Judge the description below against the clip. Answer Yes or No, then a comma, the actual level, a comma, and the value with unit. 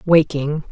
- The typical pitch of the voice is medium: Yes, medium, 155 Hz